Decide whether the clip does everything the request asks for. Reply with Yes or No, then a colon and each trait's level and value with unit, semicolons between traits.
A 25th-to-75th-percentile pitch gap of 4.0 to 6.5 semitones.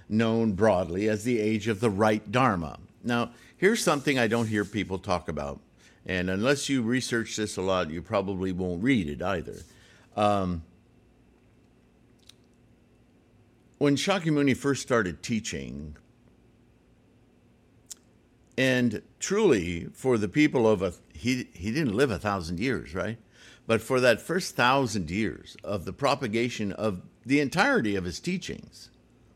Yes: average, 4.9 semitones